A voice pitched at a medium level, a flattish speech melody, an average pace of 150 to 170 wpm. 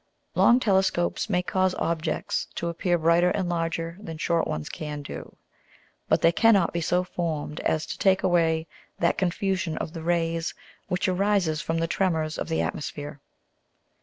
Yes: medium, 170 Hz; narrow, 2.2 semitones; average, 165 wpm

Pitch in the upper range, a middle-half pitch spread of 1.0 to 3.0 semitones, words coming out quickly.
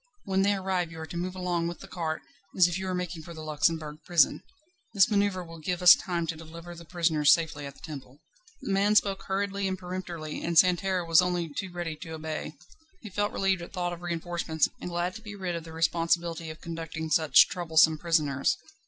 No: medium, 170 Hz; narrow, 2.4 semitones; fast, 215 wpm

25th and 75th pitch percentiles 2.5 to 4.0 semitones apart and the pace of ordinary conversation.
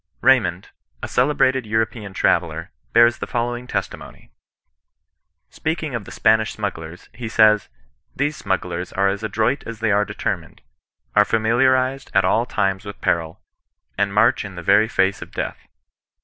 Yes: average, 3.5 semitones; average, 155 wpm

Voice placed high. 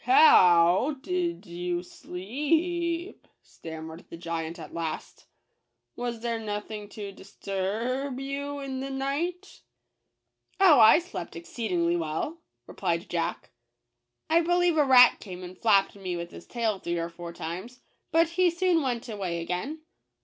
Yes: high, 230 Hz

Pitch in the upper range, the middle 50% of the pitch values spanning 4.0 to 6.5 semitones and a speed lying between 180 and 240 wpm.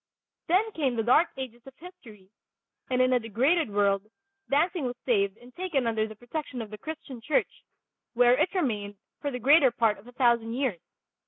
Yes: high, 245 Hz; average, 4.4 semitones; average, 185 wpm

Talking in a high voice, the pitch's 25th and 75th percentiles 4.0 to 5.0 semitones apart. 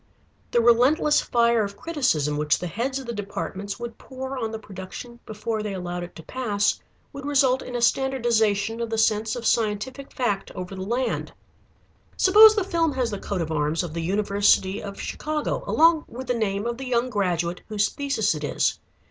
Yes: high, 225 Hz; average, 4.6 semitones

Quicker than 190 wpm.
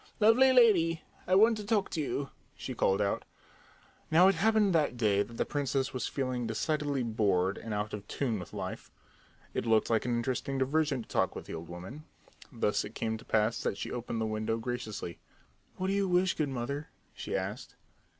Yes: average, 200 wpm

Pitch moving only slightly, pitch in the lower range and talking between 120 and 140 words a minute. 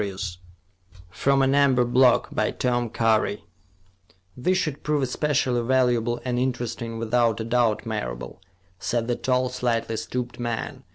Yes: narrow, 2.0 semitones; low, 120 Hz; slow, 135 wpm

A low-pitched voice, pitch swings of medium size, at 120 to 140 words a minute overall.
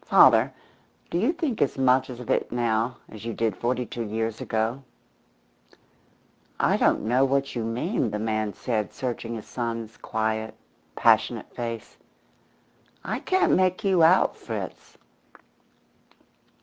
Yes: low, 120 Hz; average, 3.3 semitones; slow, 135 wpm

